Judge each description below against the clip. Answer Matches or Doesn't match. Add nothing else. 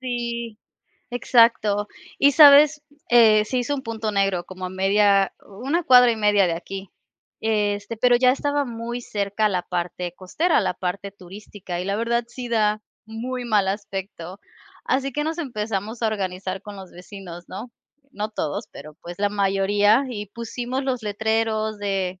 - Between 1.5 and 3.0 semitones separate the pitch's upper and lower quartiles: Doesn't match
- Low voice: Doesn't match